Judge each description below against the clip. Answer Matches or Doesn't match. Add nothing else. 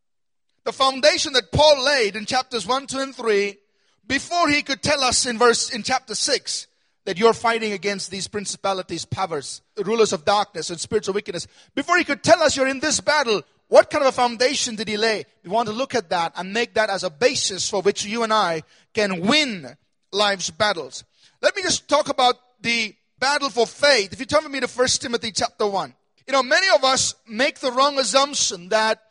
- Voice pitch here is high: Matches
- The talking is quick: Matches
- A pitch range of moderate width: Matches